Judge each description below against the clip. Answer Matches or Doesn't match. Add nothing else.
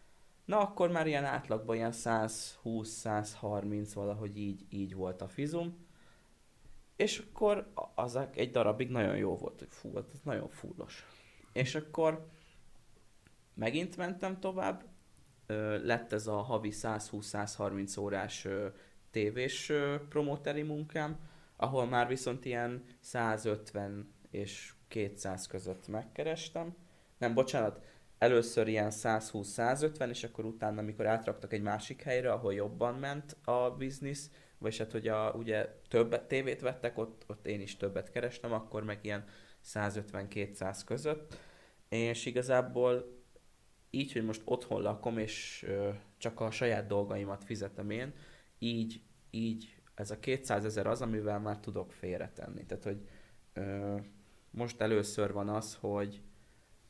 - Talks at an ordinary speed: Matches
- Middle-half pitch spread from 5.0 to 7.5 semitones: Doesn't match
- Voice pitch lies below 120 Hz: Matches